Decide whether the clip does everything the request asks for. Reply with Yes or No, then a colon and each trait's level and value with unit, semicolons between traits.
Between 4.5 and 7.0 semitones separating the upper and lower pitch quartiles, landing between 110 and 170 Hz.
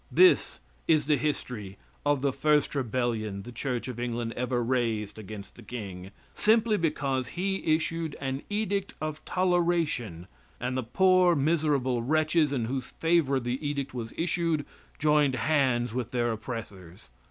Yes: average, 4.8 semitones; low, 135 Hz